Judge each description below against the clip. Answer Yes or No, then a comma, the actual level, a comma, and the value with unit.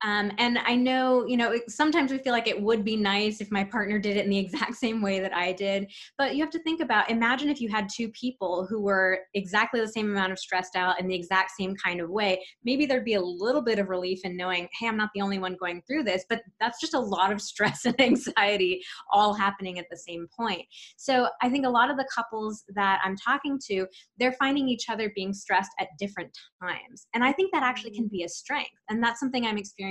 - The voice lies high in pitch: Yes, high, 215 Hz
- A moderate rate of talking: No, fast, 250 wpm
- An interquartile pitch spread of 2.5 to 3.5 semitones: No, average, 4.2 semitones